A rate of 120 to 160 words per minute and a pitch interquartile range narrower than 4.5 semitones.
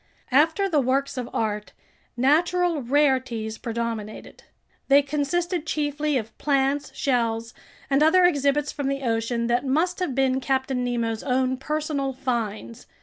Yes: slow, 135 wpm; average, 3.7 semitones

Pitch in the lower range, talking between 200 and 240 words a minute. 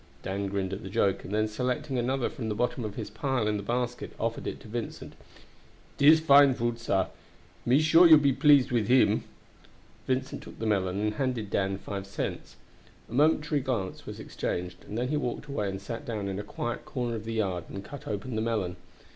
Yes: low, 115 Hz; fast, 205 wpm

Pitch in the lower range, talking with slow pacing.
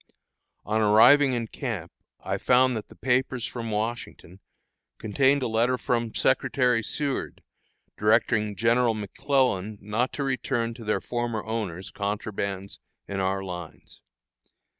Yes: low, 115 Hz; slow, 125 wpm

